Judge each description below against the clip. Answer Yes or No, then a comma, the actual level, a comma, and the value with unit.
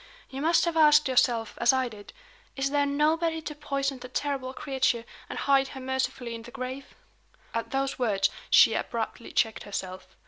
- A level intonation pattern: No, average, 3.2 semitones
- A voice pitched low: No, very high, 265 Hz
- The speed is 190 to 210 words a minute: No, average, 175 wpm